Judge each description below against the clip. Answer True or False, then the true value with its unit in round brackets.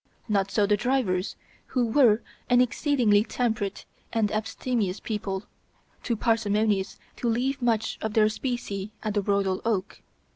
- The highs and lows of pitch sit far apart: False (3.0 semitones)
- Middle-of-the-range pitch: False (215 Hz)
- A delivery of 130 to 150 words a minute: True (140 wpm)